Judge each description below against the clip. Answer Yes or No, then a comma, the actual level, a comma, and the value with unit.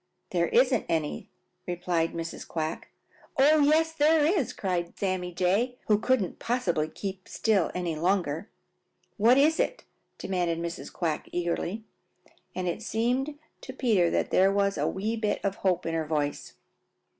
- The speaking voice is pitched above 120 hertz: Yes, high, 190 Hz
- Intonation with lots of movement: Yes, wide, 6.3 semitones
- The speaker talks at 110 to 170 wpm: Yes, average, 150 wpm